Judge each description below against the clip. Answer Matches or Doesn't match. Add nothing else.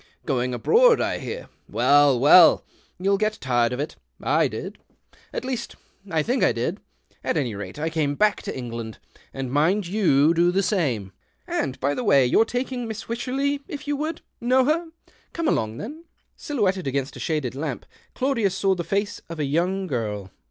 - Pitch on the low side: Doesn't match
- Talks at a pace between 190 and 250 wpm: Matches